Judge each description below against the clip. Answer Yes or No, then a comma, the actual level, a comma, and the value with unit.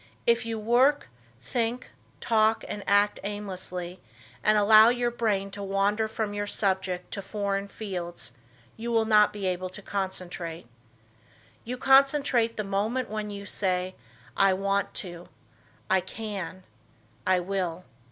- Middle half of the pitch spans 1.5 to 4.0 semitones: Yes, average, 2.9 semitones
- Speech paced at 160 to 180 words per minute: No, average, 140 wpm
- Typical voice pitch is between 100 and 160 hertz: No, high, 205 Hz